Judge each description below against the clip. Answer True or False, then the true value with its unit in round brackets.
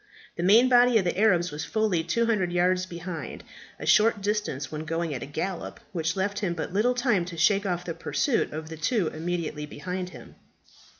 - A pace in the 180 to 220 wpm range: True (195 wpm)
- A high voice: False (180 Hz)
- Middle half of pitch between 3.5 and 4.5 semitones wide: True (4.2 semitones)